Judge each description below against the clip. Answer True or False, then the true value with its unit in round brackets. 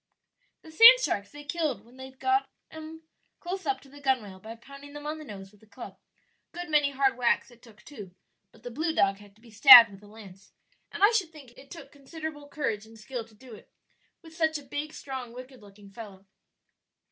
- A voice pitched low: False (265 Hz)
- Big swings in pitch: True (6.0 semitones)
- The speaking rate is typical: False (220 wpm)